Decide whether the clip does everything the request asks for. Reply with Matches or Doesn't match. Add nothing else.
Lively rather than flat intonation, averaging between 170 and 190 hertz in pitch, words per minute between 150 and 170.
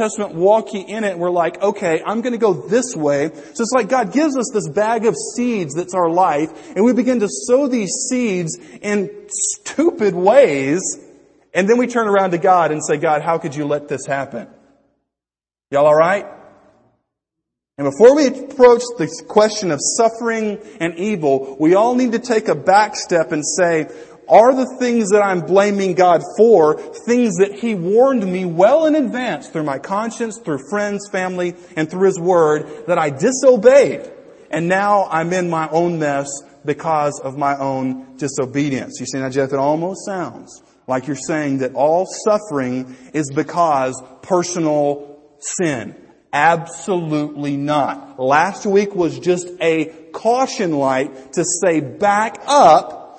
Matches